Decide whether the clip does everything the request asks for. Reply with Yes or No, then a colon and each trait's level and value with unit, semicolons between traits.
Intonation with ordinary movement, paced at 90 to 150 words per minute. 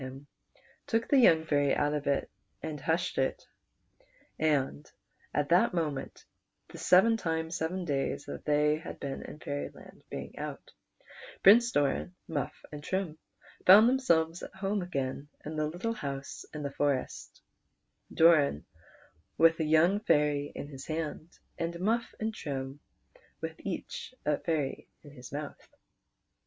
Yes: average, 3.7 semitones; average, 145 wpm